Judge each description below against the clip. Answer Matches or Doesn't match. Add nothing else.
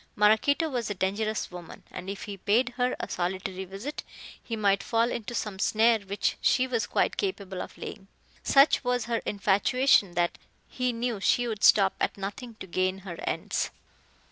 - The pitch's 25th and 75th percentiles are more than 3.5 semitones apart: Matches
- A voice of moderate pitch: Doesn't match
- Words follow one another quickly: Doesn't match